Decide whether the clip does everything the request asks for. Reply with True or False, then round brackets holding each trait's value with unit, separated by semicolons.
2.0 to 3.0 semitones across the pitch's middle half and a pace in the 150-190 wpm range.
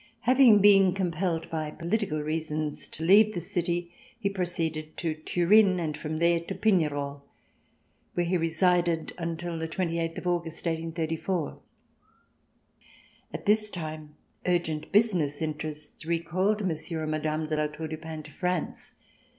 False (2.5 semitones; 140 wpm)